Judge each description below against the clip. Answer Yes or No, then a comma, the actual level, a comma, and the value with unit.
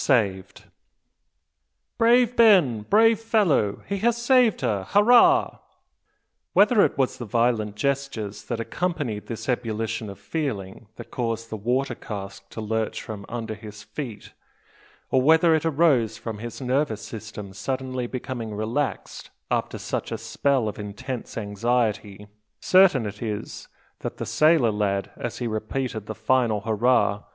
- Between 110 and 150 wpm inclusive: Yes, average, 140 wpm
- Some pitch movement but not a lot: Yes, average, 5.0 semitones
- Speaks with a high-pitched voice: No, low, 115 Hz